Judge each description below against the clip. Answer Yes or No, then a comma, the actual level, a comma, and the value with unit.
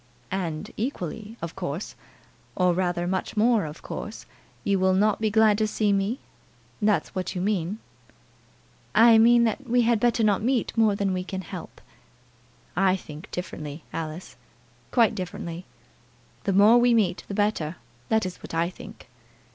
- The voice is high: Yes, high, 200 Hz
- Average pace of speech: Yes, average, 160 wpm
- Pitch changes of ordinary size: Yes, average, 3.6 semitones